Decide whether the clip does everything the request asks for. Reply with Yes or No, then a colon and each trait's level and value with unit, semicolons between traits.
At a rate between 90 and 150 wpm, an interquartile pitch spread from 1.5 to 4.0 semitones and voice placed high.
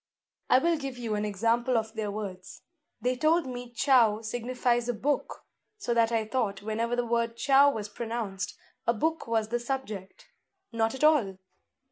No: average, 170 wpm; average, 2.7 semitones; high, 235 Hz